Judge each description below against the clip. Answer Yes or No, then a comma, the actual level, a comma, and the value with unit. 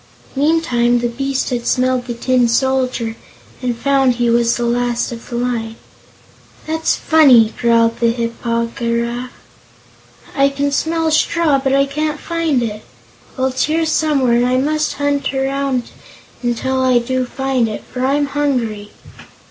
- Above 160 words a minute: No, average, 155 wpm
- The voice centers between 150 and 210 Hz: No, very high, 255 Hz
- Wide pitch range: No, average, 2.8 semitones